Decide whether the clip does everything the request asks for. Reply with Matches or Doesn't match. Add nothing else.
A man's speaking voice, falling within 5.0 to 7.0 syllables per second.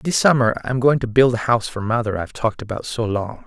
Matches